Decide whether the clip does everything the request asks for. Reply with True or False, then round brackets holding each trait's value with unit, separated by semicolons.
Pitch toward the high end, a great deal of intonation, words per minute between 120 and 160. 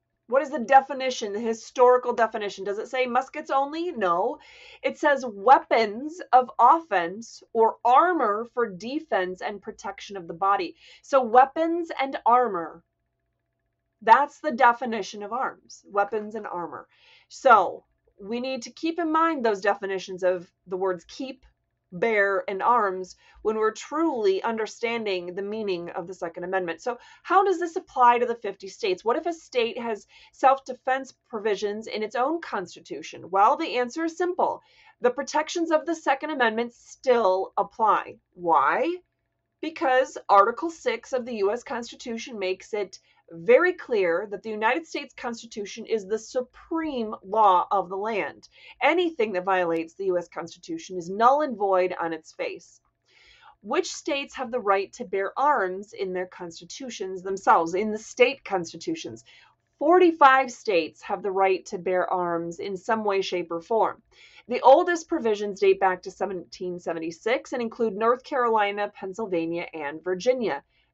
True (230 Hz; 6.6 semitones; 150 wpm)